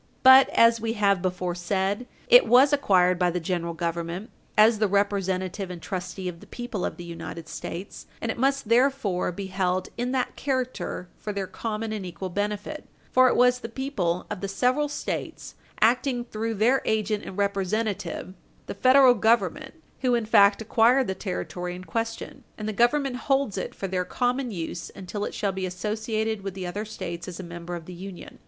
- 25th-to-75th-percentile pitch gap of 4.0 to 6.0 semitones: Yes, average, 4.7 semitones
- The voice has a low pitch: No, high, 205 Hz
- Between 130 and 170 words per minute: No, average, 190 wpm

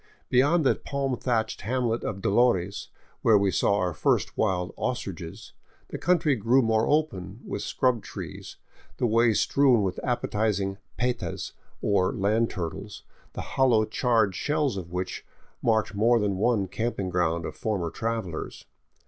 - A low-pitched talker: Yes, low, 110 Hz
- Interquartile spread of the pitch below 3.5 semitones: No, average, 4.2 semitones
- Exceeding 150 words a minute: No, average, 145 wpm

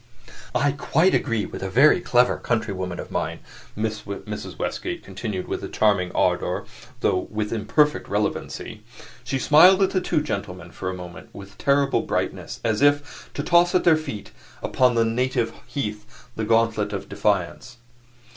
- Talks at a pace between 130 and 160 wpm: Yes, average, 155 wpm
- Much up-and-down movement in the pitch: Yes, wide, 5.7 semitones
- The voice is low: Yes, low, 115 Hz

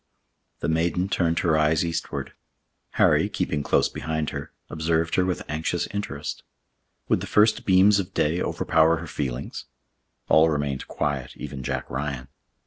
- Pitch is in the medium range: No, very low, 80 Hz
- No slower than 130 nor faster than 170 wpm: Yes, average, 145 wpm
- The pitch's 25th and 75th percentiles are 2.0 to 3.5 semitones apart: Yes, average, 3.0 semitones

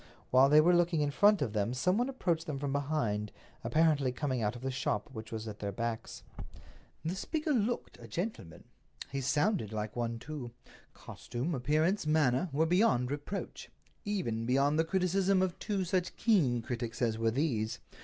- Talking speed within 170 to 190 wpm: Yes, average, 175 wpm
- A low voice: No, medium, 145 Hz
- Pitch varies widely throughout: Yes, wide, 7.0 semitones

